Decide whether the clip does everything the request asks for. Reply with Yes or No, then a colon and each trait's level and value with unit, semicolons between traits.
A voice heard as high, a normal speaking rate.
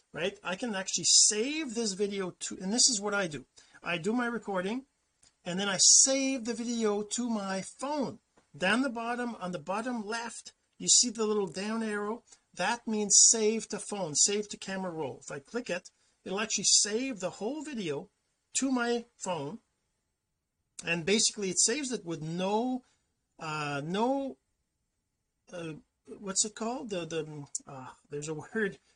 Yes: high, 210 Hz; average, 170 wpm